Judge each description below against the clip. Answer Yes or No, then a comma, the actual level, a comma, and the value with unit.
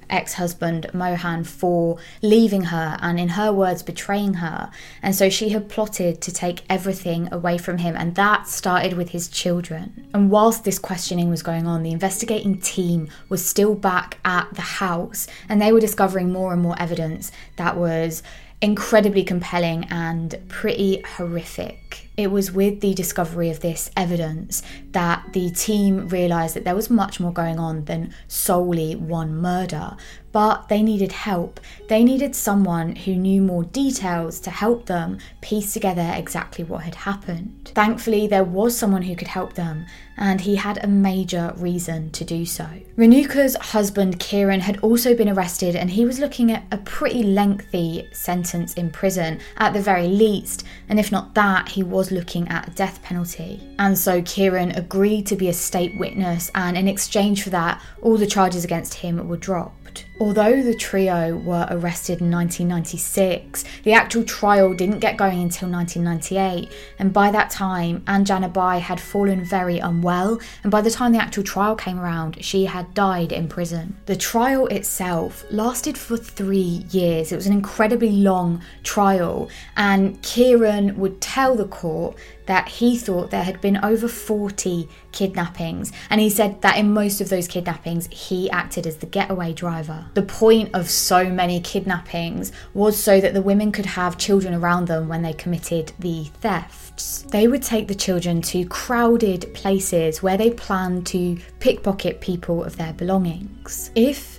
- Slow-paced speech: No, average, 170 wpm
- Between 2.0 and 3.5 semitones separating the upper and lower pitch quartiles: Yes, average, 2.9 semitones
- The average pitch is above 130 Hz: Yes, high, 190 Hz